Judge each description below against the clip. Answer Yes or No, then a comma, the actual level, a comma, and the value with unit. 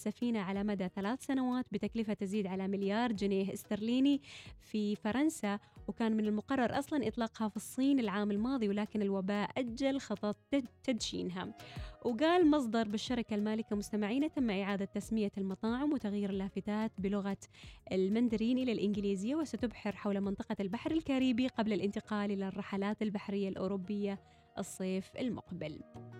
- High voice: Yes, high, 210 Hz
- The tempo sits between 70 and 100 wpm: No, average, 125 wpm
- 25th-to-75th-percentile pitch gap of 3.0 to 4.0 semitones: Yes, average, 3.3 semitones